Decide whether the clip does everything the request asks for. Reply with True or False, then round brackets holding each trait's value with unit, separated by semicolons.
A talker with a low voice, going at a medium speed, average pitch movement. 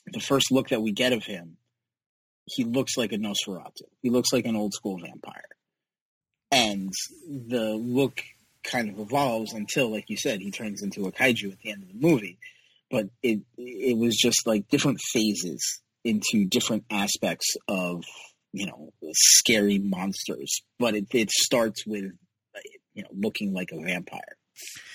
True (115 Hz; 165 wpm; 4.2 semitones)